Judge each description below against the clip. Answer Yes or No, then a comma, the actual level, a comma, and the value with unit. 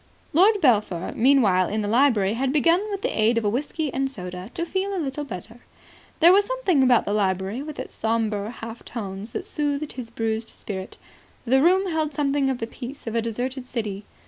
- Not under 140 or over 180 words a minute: No, average, 200 wpm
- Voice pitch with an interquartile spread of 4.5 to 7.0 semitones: Yes, wide, 5.4 semitones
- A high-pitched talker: Yes, high, 245 Hz